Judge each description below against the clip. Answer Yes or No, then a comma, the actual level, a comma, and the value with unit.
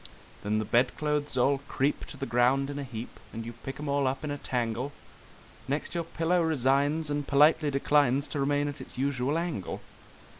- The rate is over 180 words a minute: Yes, average, 190 wpm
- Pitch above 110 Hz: Yes, medium, 140 Hz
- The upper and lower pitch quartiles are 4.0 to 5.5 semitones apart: No, average, 2.7 semitones